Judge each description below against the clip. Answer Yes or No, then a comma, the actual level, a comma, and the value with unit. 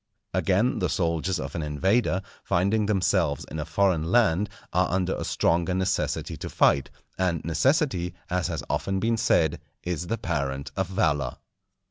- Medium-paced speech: Yes, average, 155 wpm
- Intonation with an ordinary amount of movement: Yes, average, 3.3 semitones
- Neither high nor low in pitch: No, very low, 90 Hz